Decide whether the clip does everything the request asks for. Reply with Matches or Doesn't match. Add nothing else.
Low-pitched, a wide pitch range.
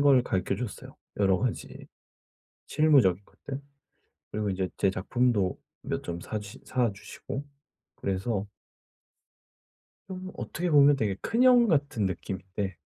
Matches